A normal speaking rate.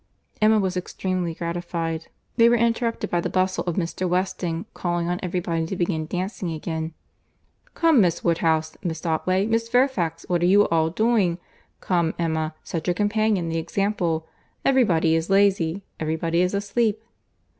Yes: average, 155 wpm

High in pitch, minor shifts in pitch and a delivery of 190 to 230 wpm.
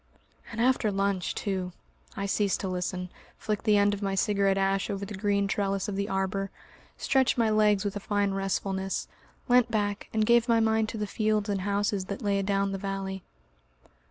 Yes: high, 200 Hz; narrow, 1.5 semitones; average, 195 wpm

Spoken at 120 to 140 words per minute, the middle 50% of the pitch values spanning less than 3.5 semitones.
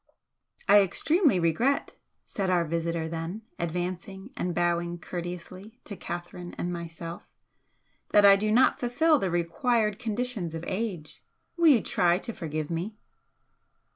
No: slow, 135 wpm; average, 4.3 semitones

